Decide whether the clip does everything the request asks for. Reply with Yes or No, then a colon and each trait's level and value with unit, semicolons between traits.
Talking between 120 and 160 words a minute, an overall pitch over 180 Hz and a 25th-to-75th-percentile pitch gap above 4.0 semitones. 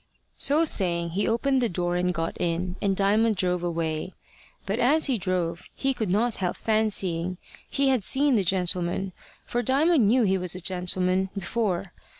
No: average, 170 wpm; high, 190 Hz; average, 4.6 semitones